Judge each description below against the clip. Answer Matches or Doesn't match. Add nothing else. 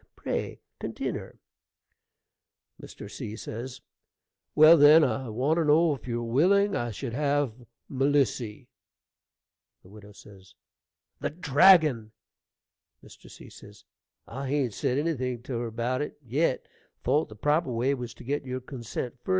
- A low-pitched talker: Matches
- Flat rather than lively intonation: Doesn't match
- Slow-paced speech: Matches